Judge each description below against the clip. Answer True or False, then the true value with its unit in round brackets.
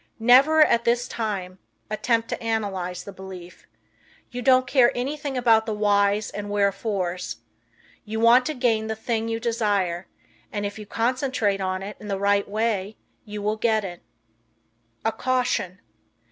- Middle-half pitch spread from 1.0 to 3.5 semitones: True (2.9 semitones)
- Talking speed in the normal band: True (155 wpm)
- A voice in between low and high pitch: False (215 Hz)